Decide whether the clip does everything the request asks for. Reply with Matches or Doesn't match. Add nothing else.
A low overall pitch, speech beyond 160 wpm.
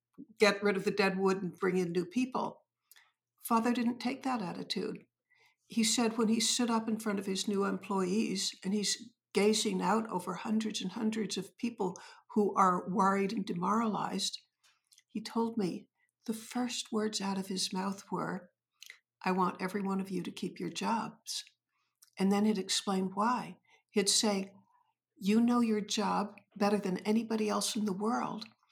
Doesn't match